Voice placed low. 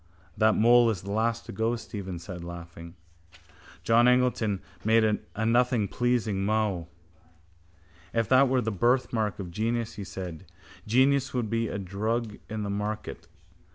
Yes: low, 110 Hz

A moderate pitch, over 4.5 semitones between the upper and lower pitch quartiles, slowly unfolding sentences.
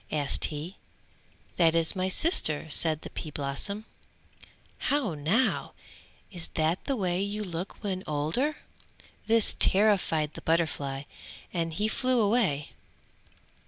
Yes: medium, 175 Hz; average, 5.3 semitones; slow, 125 wpm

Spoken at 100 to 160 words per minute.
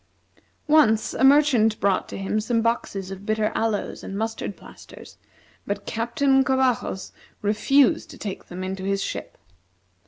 Yes: average, 145 wpm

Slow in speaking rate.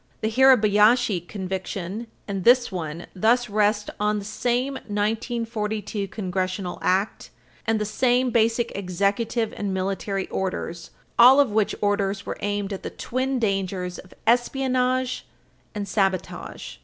Yes: slow, 130 wpm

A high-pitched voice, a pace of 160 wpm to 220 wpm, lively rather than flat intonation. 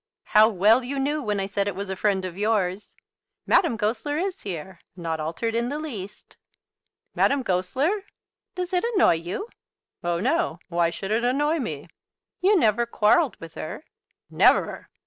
Yes: high, 215 Hz; average, 165 wpm; wide, 7.3 semitones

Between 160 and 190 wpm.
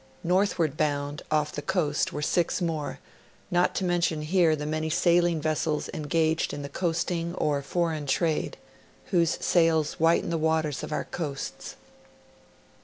No: average, 140 wpm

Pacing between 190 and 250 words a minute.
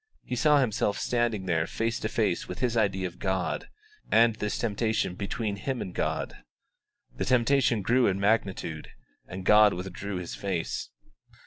No: average, 155 wpm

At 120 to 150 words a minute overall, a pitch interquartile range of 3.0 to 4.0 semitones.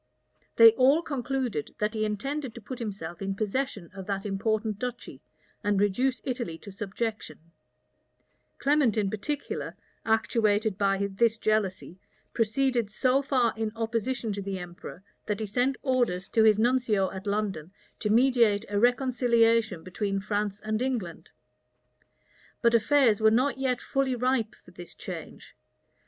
Yes: average, 145 wpm; average, 3.7 semitones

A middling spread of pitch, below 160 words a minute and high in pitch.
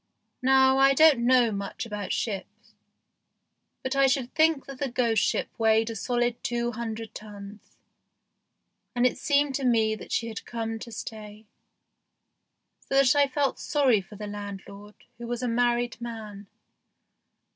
Yes: average, 3.3 semitones; average, 150 wpm; high, 235 Hz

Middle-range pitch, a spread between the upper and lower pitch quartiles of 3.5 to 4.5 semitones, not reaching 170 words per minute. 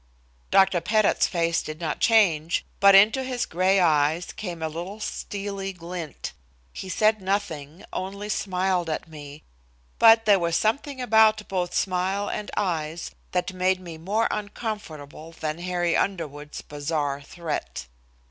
Yes: medium, 180 Hz; average, 4.0 semitones; average, 140 wpm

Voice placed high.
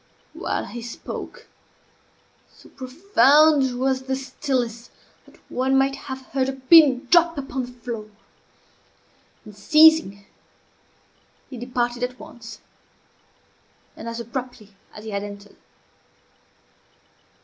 Yes: very high, 255 Hz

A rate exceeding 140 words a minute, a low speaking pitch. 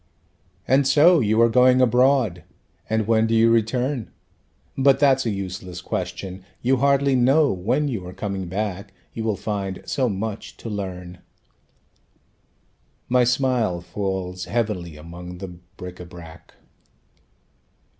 No: slow, 135 wpm; low, 110 Hz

